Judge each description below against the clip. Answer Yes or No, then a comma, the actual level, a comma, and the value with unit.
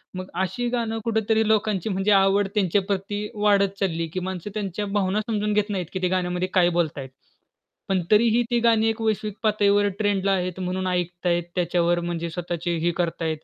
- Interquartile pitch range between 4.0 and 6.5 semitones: No, average, 2.9 semitones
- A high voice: Yes, high, 195 Hz